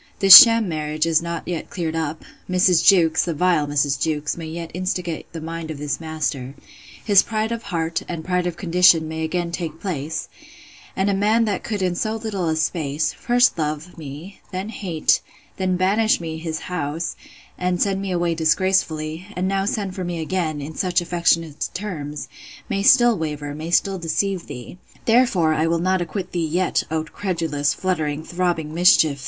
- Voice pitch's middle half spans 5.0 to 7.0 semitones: No, average, 2.9 semitones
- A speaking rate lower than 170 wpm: No, average, 180 wpm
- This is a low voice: No, medium, 170 Hz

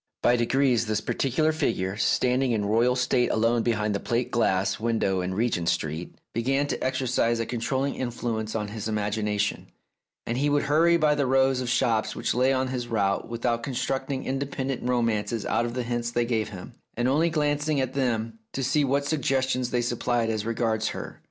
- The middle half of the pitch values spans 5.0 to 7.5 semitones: No, average, 3.2 semitones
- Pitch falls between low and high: No, low, 120 Hz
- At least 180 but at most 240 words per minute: Yes, average, 190 wpm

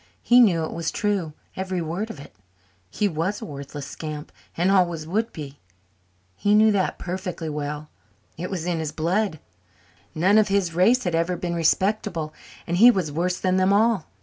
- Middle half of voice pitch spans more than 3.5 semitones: Yes, average, 3.9 semitones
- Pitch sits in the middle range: Yes, medium, 180 Hz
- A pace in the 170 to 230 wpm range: Yes, average, 180 wpm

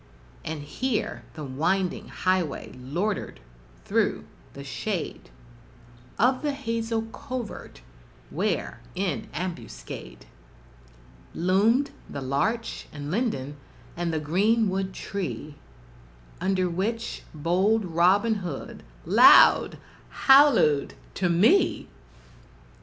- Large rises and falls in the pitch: Yes, wide, 6.2 semitones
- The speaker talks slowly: Yes, slow, 90 wpm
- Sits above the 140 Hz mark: Yes, medium, 185 Hz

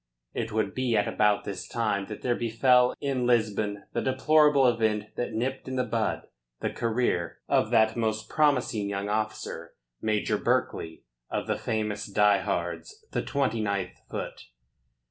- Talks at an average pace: Yes, average, 150 wpm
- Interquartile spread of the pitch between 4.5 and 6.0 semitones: No, average, 3.2 semitones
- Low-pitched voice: Yes, low, 110 Hz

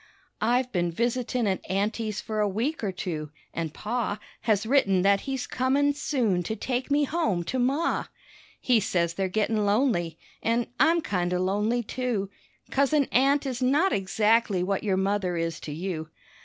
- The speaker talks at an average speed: Yes, average, 170 wpm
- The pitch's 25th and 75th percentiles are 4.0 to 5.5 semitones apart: Yes, average, 5.2 semitones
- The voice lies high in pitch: Yes, high, 215 Hz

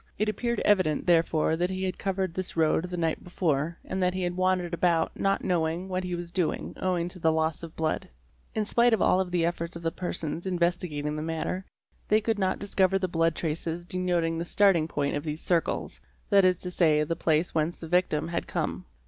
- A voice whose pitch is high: No, medium, 175 Hz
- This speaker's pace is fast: Yes, fast, 215 wpm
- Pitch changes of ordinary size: No, narrow, 2.3 semitones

